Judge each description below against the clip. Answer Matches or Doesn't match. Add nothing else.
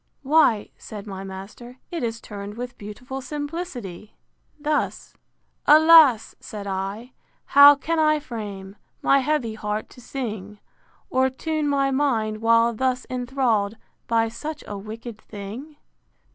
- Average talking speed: Doesn't match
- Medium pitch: Doesn't match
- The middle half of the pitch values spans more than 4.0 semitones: Matches